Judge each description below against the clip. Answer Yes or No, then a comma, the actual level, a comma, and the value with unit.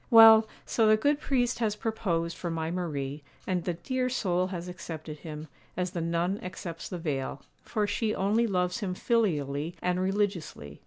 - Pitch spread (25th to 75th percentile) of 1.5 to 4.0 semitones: No, average, 4.6 semitones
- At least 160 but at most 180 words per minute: Yes, average, 170 wpm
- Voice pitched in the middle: Yes, medium, 180 Hz